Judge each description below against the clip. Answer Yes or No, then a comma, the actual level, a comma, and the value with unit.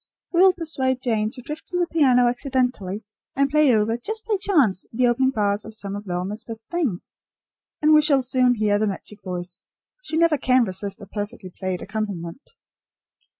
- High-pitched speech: Yes, high, 240 Hz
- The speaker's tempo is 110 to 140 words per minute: No, average, 185 wpm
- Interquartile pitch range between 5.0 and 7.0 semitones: Yes, wide, 5.4 semitones